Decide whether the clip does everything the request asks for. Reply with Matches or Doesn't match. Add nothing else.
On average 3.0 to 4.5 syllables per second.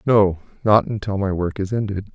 Doesn't match